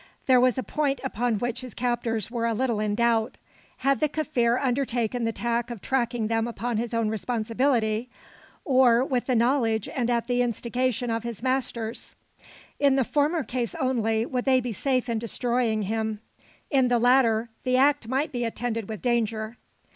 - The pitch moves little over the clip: Yes, narrow, 2.1 semitones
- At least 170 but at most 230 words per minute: Yes, average, 175 wpm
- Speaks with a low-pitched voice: No, high, 240 Hz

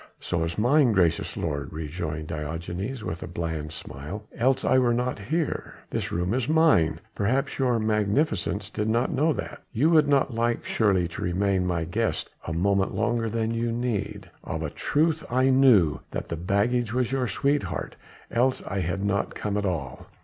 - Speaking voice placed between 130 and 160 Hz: No, low, 105 Hz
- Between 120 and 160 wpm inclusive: No, average, 180 wpm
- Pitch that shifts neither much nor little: No, wide, 6.4 semitones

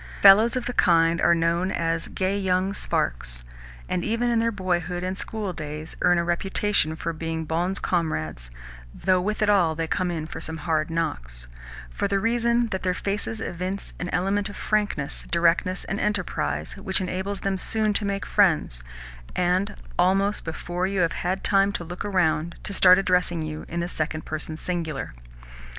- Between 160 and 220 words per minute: Yes, average, 175 wpm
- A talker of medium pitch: Yes, medium, 180 Hz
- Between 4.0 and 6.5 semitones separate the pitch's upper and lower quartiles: No, average, 3.3 semitones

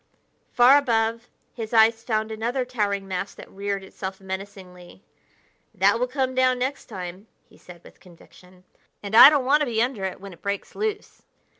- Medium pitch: No, high, 220 Hz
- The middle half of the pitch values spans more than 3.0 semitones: Yes, average, 4.5 semitones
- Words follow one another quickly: No, average, 175 wpm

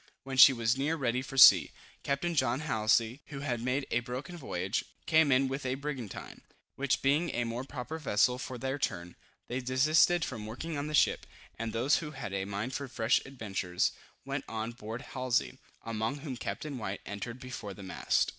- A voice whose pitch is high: No, low, 130 Hz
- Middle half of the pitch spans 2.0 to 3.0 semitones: No, average, 3.7 semitones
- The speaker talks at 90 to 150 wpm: No, average, 190 wpm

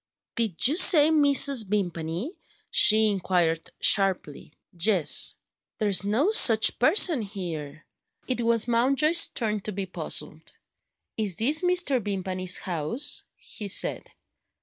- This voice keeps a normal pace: No, slow, 115 wpm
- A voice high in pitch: Yes, high, 215 Hz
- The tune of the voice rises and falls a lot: Yes, wide, 6.5 semitones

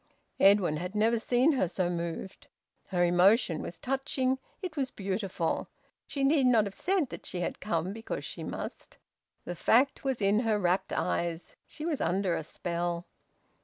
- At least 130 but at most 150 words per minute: No, average, 165 wpm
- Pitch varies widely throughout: Yes, wide, 6.5 semitones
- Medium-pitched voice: No, high, 200 Hz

